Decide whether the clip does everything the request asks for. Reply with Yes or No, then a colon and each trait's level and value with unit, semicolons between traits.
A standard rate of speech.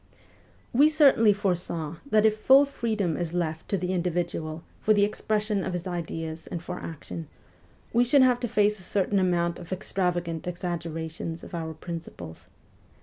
Yes: average, 160 wpm